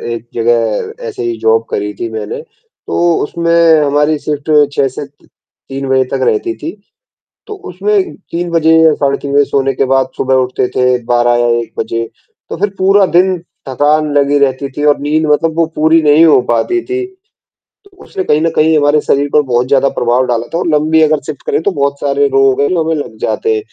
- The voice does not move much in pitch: No, average, 4.1 semitones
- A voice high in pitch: No, medium, 150 Hz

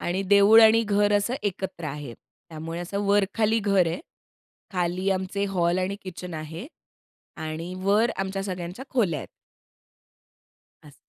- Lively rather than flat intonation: No, average, 3.1 semitones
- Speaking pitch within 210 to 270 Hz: No, high, 190 Hz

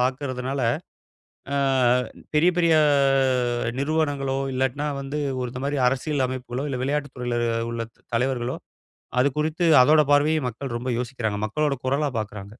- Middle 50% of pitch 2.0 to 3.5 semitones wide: Yes, average, 2.9 semitones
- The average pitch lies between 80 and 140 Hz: Yes, low, 135 Hz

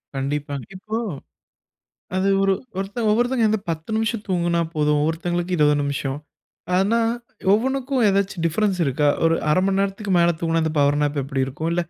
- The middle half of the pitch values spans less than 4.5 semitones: No, wide, 5.5 semitones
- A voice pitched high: No, medium, 175 Hz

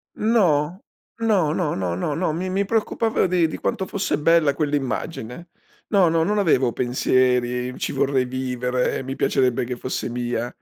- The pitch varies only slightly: No, wide, 6.2 semitones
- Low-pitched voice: No, medium, 145 Hz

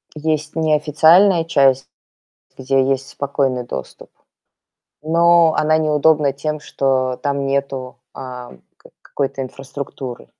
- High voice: No, medium, 140 Hz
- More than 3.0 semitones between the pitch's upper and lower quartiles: No, average, 2.7 semitones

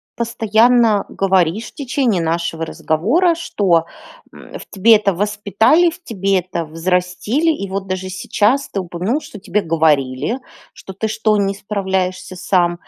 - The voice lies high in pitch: Yes, high, 195 Hz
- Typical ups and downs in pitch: Yes, average, 3.8 semitones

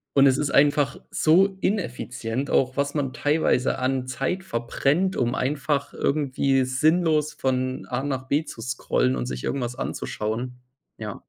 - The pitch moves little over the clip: No, average, 3.1 semitones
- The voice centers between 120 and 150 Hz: Yes, low, 135 Hz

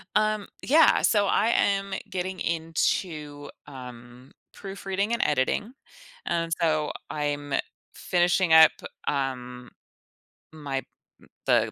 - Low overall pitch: No, medium, 160 Hz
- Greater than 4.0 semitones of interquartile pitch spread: Yes, average, 5.3 semitones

